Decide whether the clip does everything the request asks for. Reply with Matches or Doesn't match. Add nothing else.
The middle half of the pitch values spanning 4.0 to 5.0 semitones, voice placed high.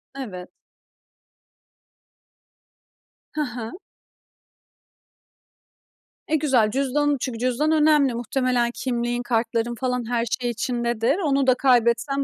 Doesn't match